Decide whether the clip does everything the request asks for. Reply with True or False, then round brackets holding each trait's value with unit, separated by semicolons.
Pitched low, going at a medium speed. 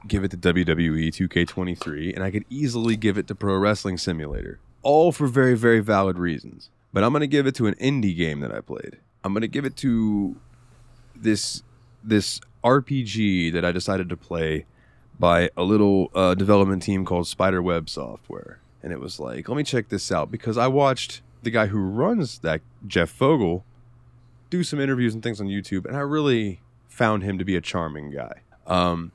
True (105 Hz; 195 wpm)